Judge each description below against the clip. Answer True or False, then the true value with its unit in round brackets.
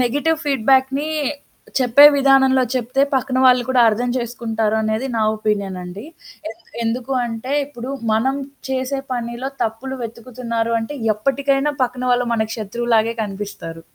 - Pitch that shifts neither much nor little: True (3.1 semitones)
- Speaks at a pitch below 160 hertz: False (240 Hz)